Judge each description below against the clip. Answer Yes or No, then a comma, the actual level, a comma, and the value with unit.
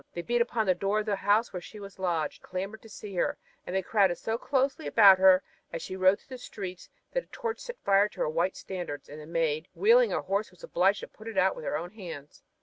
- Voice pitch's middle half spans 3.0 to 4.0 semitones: Yes, average, 3.7 semitones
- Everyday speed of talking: No, fast, 260 wpm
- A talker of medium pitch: No, high, 195 Hz